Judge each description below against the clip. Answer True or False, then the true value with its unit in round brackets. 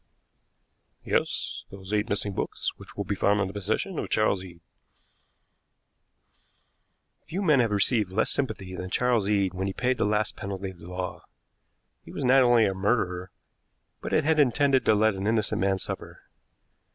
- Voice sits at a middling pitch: False (105 Hz)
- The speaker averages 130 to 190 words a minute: True (170 wpm)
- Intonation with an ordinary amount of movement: True (4.2 semitones)